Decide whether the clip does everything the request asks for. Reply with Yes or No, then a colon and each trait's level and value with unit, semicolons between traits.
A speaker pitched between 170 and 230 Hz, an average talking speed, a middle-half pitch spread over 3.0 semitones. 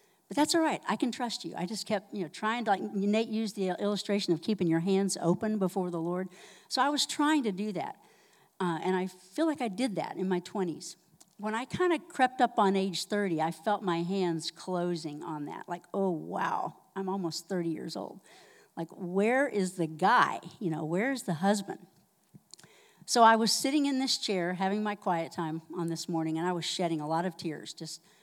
No: high, 190 Hz; fast, 220 wpm; average, 3.9 semitones